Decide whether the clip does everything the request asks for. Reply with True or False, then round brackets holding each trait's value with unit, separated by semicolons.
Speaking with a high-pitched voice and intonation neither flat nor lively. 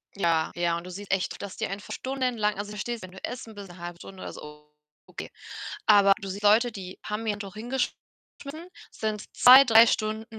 True (205 Hz; 3.1 semitones)